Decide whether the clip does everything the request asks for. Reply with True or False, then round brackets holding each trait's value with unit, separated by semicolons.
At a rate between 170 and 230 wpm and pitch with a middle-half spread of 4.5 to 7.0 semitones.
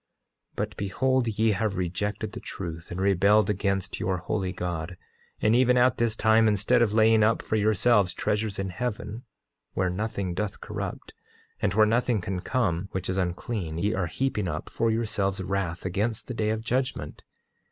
False (175 wpm; 3.2 semitones)